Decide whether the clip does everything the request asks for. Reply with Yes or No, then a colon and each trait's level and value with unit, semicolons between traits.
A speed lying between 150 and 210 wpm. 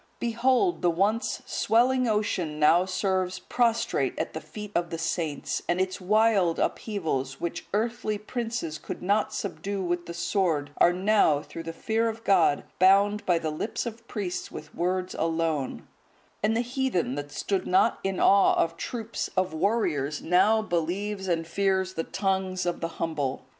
Yes: average, 165 wpm